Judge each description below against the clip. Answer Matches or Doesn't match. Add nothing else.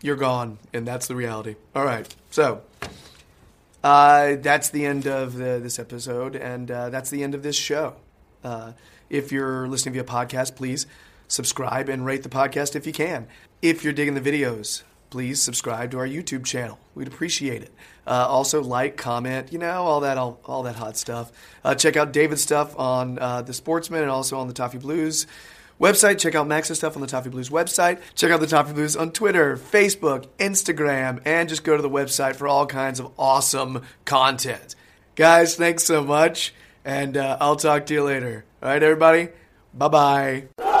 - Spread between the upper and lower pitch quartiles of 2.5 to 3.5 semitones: Matches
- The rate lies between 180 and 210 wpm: Matches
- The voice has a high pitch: Doesn't match